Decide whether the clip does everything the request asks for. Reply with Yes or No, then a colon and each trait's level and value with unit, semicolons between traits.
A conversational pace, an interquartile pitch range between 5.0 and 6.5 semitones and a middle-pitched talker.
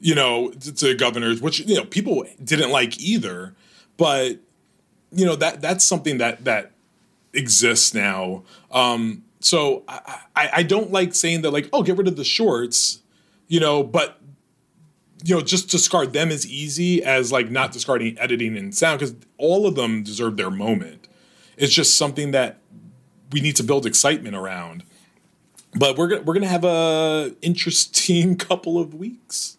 Yes: average, 165 wpm; wide, 5.6 semitones; medium, 160 Hz